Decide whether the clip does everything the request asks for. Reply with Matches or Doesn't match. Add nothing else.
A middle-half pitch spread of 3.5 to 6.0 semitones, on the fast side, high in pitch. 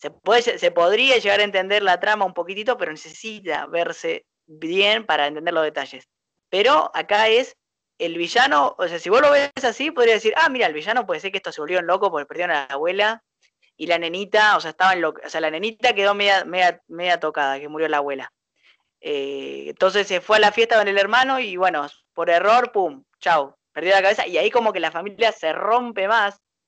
Matches